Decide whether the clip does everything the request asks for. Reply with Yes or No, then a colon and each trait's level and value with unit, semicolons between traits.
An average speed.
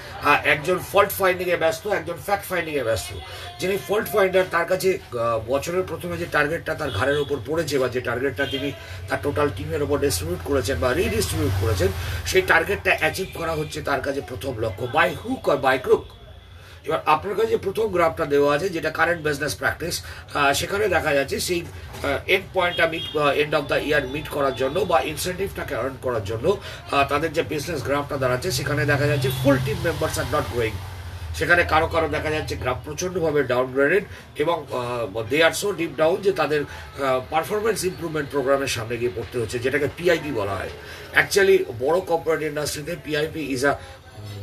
No: fast, 170 wpm